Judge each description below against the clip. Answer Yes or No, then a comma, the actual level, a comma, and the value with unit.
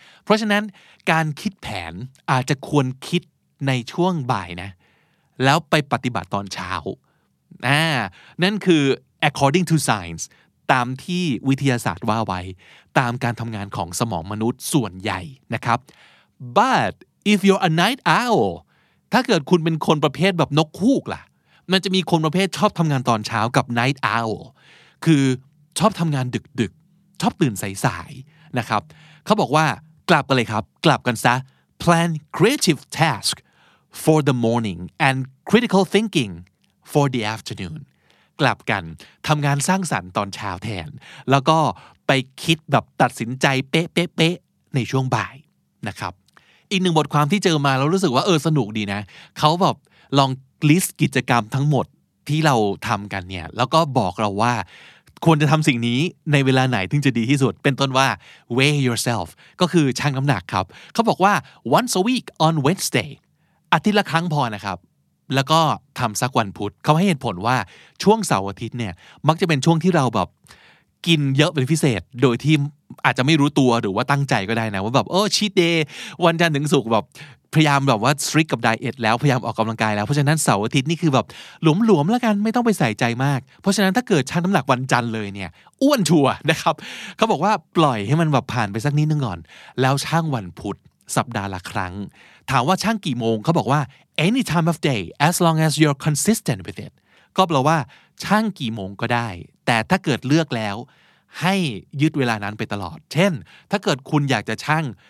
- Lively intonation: Yes, wide, 5.9 semitones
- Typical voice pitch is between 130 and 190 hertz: Yes, medium, 140 Hz